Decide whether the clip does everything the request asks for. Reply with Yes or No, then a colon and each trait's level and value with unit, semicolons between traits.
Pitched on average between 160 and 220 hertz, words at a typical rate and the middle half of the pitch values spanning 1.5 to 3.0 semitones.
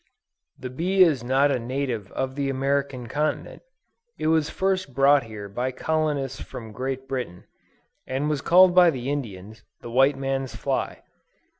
No: low, 135 Hz; average, 155 wpm; average, 2.7 semitones